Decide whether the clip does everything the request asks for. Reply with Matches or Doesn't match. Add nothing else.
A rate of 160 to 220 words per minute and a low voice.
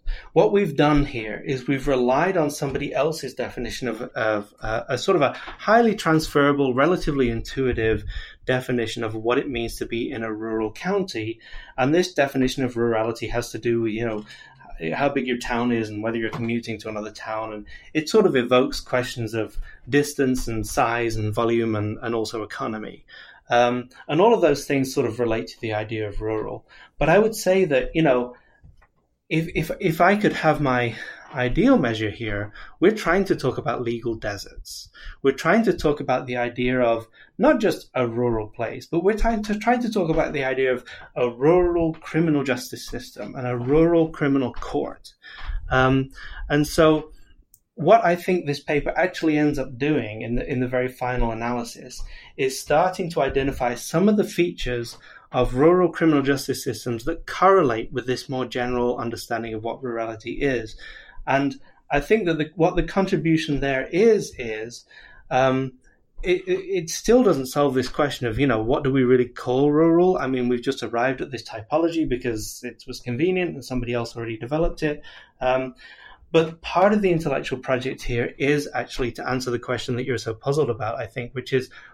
Matches